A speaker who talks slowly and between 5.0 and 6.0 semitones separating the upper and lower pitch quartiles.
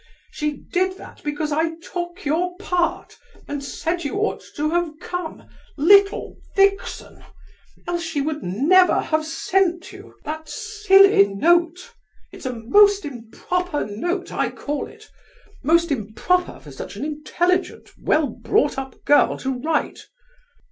No: slow, 130 wpm; average, 3.8 semitones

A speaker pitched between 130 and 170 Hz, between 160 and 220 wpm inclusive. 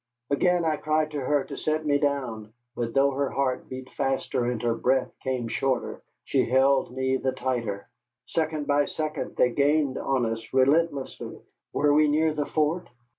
Yes: medium, 140 Hz; average, 175 wpm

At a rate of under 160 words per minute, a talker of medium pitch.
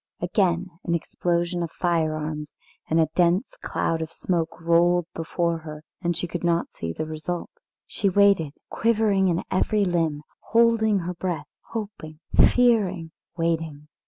Yes: average, 140 wpm; medium, 170 Hz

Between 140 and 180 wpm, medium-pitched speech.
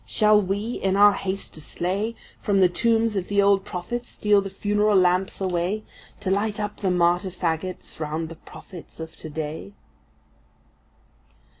No: average, 160 wpm; high, 195 Hz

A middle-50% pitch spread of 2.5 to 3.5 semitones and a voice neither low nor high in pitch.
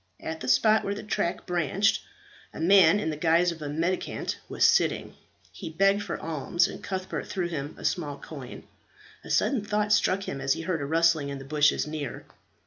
No: average, 4.4 semitones; medium, 165 Hz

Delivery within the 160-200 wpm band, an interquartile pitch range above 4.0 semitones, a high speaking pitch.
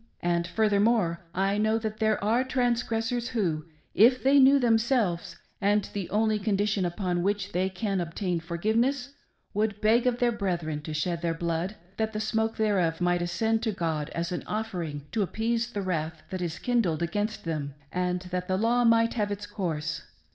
Yes: average, 175 wpm; average, 4.5 semitones; high, 200 Hz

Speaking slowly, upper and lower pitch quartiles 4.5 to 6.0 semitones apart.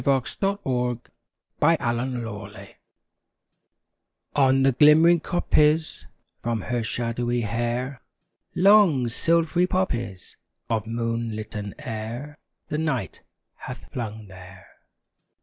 Yes: slow, 95 wpm; average, 4.8 semitones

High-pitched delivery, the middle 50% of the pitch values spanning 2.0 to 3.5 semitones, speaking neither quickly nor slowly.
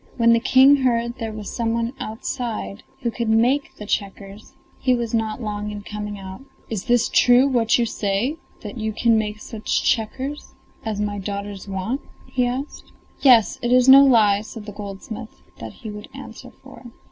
Yes: high, 225 Hz; average, 2.8 semitones; average, 180 wpm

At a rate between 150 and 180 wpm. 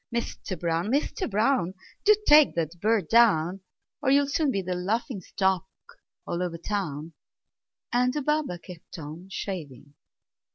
No: average, 140 wpm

